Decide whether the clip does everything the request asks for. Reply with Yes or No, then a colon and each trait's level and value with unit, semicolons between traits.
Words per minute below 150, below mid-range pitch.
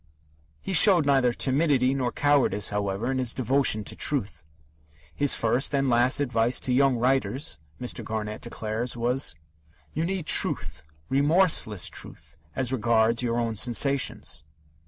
Yes: average, 140 wpm; low, 125 Hz